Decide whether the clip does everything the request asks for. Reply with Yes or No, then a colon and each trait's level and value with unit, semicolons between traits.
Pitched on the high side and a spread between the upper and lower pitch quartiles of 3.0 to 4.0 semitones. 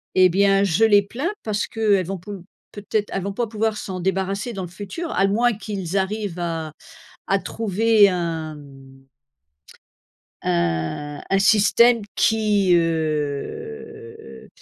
No: high, 195 Hz; average, 4.4 semitones